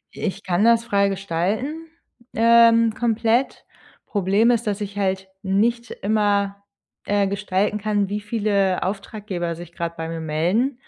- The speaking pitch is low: No, high, 205 Hz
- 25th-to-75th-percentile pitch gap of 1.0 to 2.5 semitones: No, average, 2.9 semitones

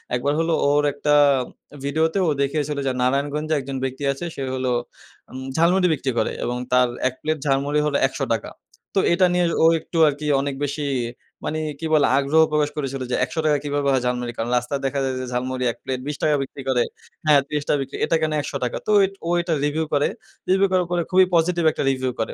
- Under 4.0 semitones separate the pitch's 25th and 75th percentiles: Yes, average, 3.0 semitones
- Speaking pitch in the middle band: Yes, medium, 145 Hz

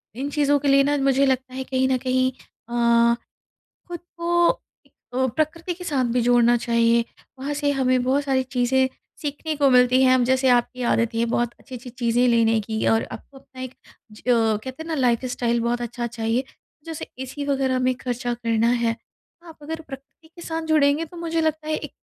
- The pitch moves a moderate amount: Yes, average, 3.1 semitones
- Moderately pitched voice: No, very high, 255 Hz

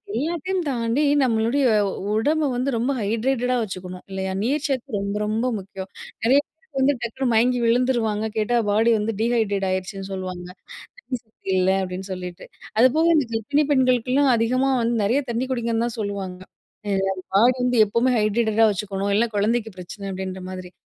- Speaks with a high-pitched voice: Yes, high, 230 Hz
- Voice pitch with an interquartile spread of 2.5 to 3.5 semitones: No, average, 4.2 semitones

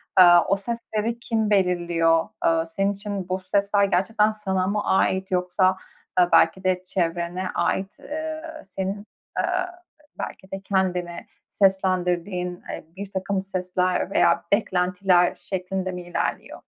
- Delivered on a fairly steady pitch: Yes, narrow, 1.8 semitones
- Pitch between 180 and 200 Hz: Yes, high, 190 Hz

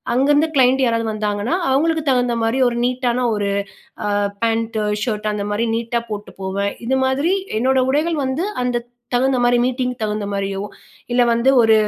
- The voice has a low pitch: No, high, 240 Hz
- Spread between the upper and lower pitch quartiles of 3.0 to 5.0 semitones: Yes, average, 3.6 semitones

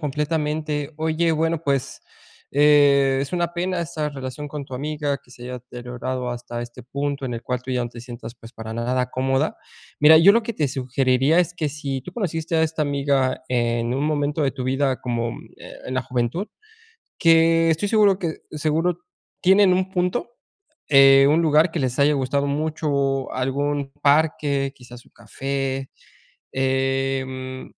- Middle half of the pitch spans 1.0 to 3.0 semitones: No, average, 3.4 semitones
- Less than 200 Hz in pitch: Yes, medium, 140 Hz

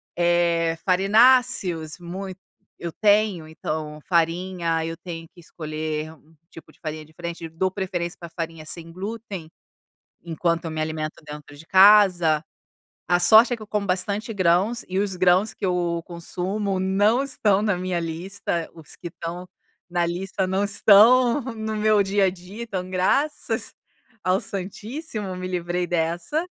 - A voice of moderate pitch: Yes, medium, 180 Hz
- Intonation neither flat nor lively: Yes, average, 3.4 semitones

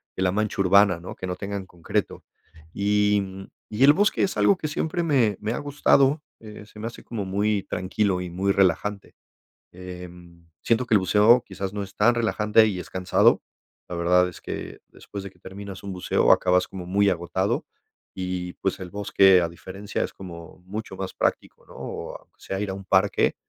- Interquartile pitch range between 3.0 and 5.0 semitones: No, narrow, 2.5 semitones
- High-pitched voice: No, low, 100 Hz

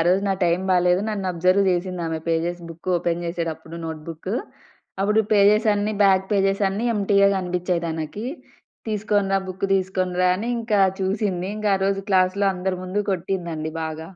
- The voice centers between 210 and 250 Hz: No, medium, 185 Hz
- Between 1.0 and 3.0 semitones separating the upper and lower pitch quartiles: Yes, narrow, 2.4 semitones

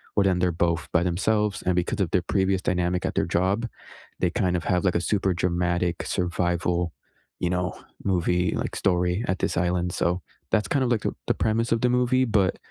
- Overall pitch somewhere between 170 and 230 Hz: No, very low, 90 Hz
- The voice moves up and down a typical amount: No, narrow, 2.3 semitones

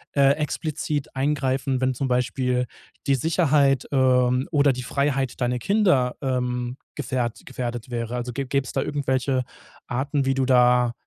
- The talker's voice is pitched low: Yes, low, 130 Hz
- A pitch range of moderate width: No, narrow, 2.0 semitones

